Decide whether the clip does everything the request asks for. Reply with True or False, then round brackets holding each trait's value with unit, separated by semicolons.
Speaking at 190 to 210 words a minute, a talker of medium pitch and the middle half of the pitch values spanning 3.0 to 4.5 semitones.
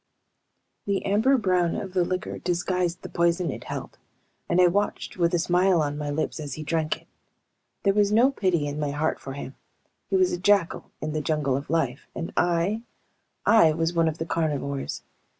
True (195 wpm; 170 Hz; 3.4 semitones)